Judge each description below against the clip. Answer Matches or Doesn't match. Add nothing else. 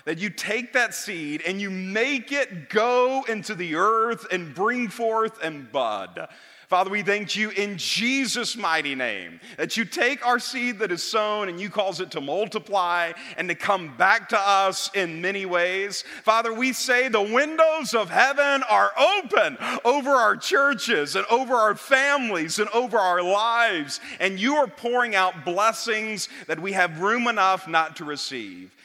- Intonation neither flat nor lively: Matches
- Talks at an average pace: Matches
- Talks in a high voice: Matches